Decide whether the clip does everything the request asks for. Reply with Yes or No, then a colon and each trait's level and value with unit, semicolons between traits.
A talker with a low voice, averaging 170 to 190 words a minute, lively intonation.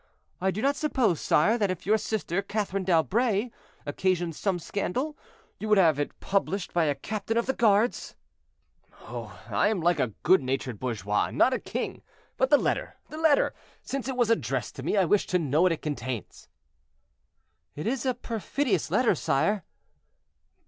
No: high, 195 Hz; average, 175 wpm; wide, 6.5 semitones